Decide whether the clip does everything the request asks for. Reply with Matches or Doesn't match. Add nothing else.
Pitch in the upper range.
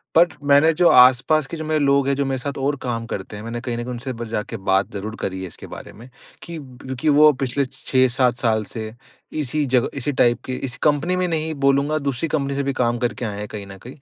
Doesn't match